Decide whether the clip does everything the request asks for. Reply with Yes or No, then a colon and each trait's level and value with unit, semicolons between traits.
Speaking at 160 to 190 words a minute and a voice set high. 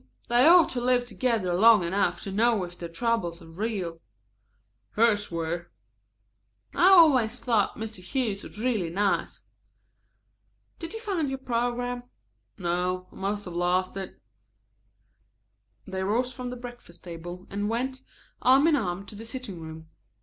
No: average, 150 wpm; high, 215 Hz